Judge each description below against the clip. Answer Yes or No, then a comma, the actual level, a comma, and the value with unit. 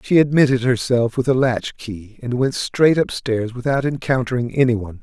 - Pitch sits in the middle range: No, low, 125 Hz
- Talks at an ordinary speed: Yes, average, 165 wpm